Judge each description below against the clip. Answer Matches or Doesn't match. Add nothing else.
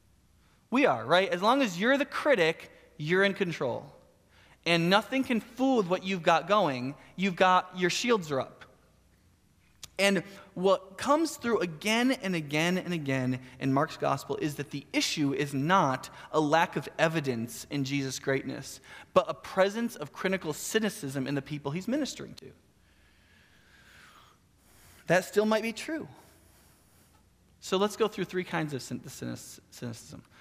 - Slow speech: Doesn't match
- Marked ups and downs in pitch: Matches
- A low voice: Doesn't match